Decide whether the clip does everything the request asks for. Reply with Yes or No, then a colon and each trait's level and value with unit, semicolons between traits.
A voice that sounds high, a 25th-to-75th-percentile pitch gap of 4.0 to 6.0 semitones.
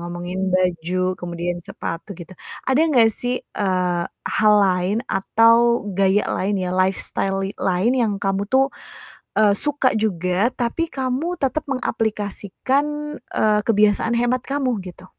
Yes: high, 205 Hz; average, 4.6 semitones